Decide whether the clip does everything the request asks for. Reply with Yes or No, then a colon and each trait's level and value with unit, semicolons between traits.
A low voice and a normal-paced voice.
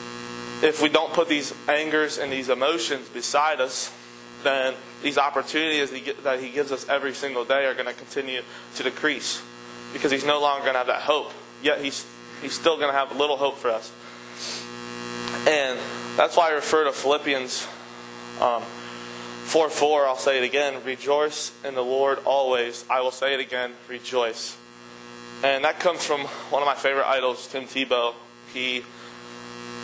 Yes: low, 125 Hz; average, 170 wpm